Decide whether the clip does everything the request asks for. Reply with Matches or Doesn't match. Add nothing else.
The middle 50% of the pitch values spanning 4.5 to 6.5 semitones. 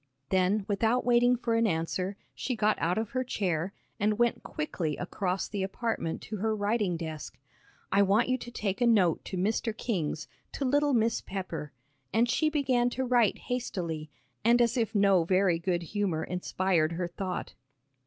Matches